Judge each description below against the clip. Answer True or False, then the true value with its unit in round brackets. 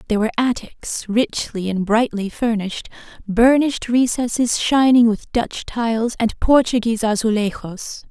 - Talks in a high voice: True (230 Hz)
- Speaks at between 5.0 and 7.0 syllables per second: False (4.8 syllables/s)